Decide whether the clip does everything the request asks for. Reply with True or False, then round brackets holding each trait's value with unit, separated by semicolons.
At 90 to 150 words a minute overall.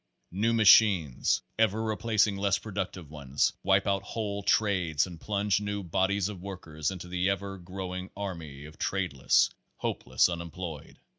True (145 wpm)